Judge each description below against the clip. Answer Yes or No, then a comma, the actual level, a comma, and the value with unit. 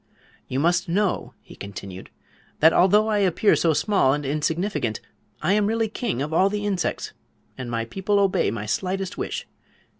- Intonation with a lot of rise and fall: Yes, wide, 6.7 semitones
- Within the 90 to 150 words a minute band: No, average, 170 wpm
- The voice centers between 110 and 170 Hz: No, medium, 180 Hz